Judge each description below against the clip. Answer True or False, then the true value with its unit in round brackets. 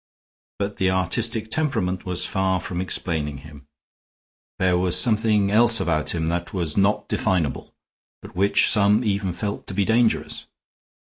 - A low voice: True (95 Hz)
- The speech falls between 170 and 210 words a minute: False (145 wpm)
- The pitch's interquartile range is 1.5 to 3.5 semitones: True (3.2 semitones)